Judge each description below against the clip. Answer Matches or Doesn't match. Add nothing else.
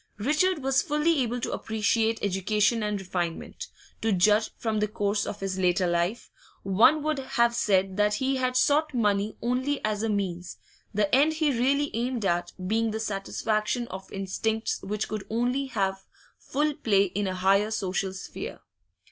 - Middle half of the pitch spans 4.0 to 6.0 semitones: Matches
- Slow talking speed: Doesn't match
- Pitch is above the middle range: Matches